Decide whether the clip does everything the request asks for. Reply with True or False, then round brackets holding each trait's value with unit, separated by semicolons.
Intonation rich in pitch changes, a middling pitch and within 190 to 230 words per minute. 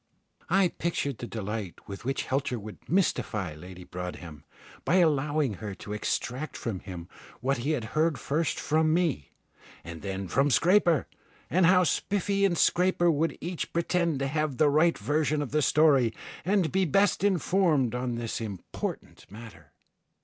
False (7.5 semitones; 145 Hz; 155 wpm)